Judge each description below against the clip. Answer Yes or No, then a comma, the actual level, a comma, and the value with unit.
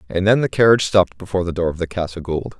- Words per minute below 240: No, fast, 275 wpm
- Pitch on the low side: Yes, very low, 90 Hz